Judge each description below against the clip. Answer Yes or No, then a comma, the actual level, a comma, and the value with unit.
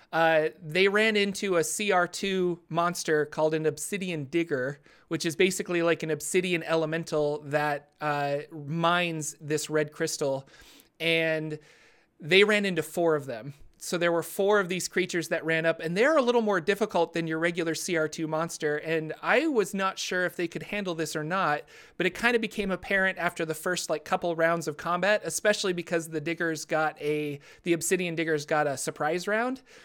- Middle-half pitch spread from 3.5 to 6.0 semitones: No, average, 2.9 semitones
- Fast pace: No, average, 185 wpm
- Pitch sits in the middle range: Yes, medium, 165 Hz